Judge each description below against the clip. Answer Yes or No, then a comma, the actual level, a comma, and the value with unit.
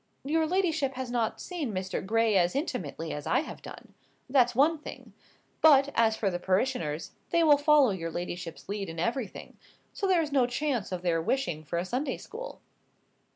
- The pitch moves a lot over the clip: Yes, wide, 8.0 semitones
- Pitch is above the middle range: Yes, high, 245 Hz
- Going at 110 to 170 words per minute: No, average, 185 wpm